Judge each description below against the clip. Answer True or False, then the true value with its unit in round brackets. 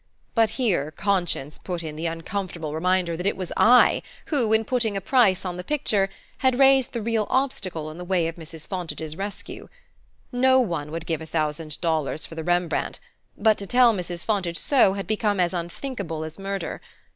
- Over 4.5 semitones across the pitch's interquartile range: True (5.0 semitones)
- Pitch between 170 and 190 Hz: True (185 Hz)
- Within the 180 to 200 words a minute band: True (190 wpm)